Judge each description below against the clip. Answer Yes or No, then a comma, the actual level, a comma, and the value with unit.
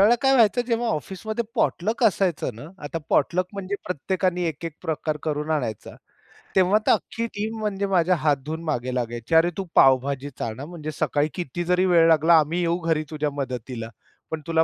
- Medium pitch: Yes, medium, 165 Hz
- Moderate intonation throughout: Yes, average, 4.5 semitones